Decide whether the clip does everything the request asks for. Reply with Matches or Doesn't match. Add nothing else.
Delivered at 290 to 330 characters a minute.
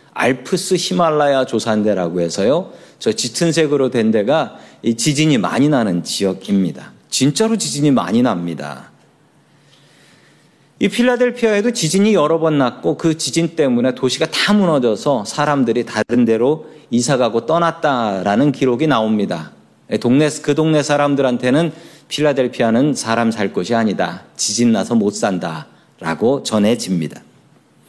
Matches